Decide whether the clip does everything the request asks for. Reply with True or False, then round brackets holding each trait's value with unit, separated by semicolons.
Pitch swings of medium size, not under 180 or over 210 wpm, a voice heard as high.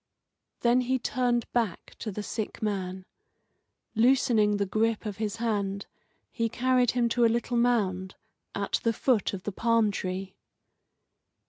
False (3.1 semitones; 145 wpm; 225 Hz)